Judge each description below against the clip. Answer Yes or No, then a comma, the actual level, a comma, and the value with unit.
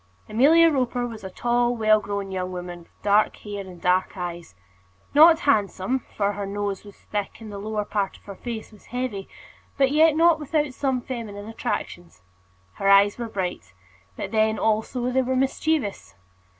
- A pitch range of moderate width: Yes, average, 4.2 semitones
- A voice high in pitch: Yes, high, 215 Hz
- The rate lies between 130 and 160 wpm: No, average, 175 wpm